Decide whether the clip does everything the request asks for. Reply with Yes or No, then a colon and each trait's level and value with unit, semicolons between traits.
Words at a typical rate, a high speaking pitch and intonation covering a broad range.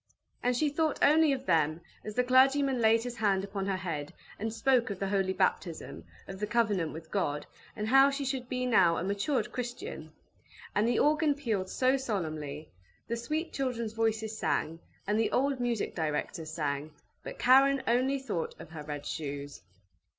Yes: average, 180 wpm; high, 220 Hz; wide, 7.3 semitones